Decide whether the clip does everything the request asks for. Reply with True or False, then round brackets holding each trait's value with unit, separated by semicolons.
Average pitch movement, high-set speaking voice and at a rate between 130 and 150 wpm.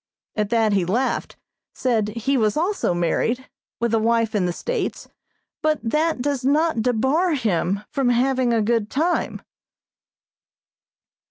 True (4.4 semitones; 235 Hz; 140 wpm)